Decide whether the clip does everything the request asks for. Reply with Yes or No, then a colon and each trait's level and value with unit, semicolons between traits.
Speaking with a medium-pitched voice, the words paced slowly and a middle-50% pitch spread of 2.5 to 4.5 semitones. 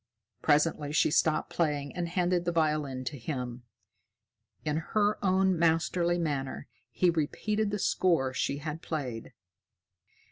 Yes: medium, 160 Hz; slow, 130 wpm; average, 3.5 semitones